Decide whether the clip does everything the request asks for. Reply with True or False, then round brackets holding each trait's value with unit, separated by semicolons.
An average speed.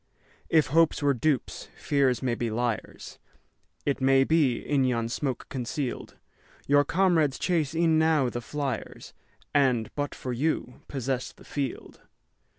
False (125 wpm)